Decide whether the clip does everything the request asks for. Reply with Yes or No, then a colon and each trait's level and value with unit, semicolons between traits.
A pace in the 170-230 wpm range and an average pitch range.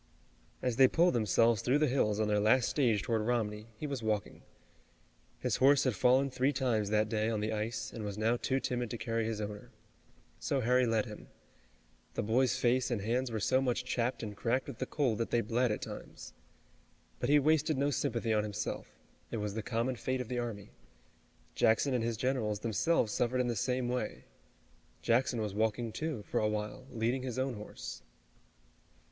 Yes: average, 195 wpm; average, 3.1 semitones